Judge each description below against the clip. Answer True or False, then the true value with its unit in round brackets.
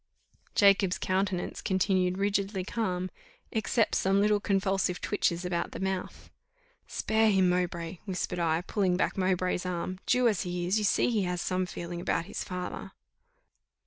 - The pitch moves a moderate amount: False (1.9 semitones)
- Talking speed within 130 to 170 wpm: True (150 wpm)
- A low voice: False (185 Hz)